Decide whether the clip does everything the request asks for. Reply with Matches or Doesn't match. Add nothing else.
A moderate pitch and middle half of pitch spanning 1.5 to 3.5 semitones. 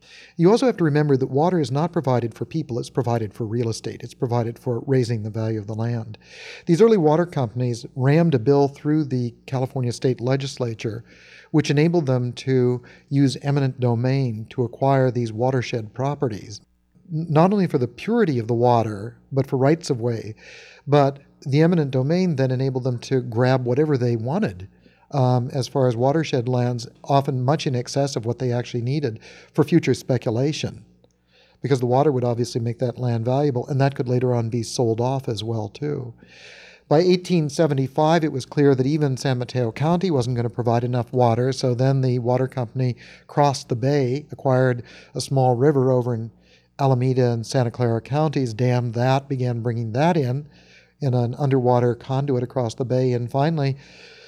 Doesn't match